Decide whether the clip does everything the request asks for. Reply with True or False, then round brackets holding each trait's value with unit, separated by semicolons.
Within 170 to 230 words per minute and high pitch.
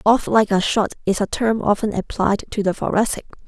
True (205 wpm; 210 Hz)